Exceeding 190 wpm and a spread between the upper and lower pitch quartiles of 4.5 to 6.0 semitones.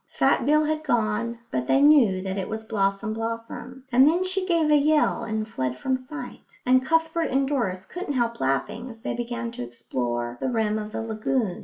Yes: average, 200 wpm; average, 5.1 semitones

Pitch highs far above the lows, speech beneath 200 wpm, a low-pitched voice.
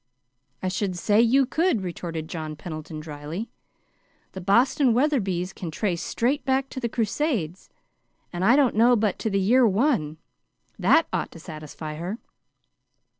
No: wide, 6.7 semitones; average, 150 wpm; high, 195 Hz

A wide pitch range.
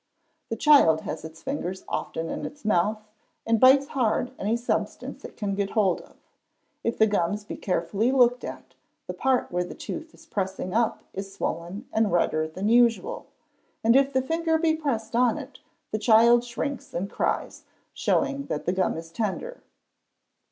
Yes: wide, 5.7 semitones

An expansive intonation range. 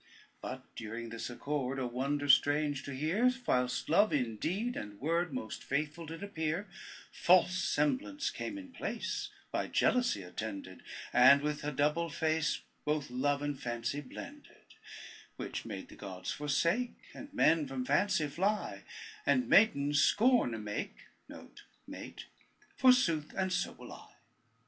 Yes: wide, 6.1 semitones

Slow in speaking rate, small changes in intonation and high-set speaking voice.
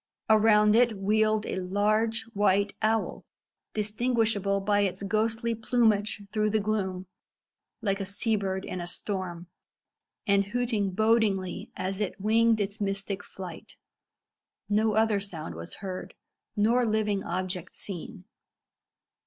Yes: slow, 125 wpm; narrow, 2.1 semitones; high, 205 Hz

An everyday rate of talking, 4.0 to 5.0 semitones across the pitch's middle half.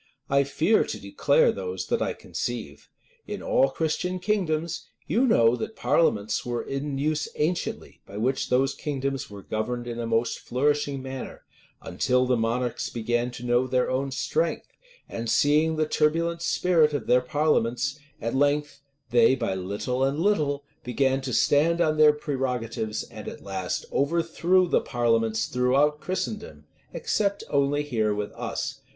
Yes: average, 155 wpm; average, 4.4 semitones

